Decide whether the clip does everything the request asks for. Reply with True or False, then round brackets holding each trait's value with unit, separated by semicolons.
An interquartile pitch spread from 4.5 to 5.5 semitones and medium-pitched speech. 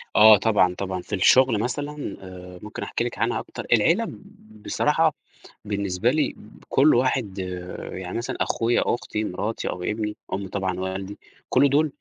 False (5.1 semitones; 105 Hz)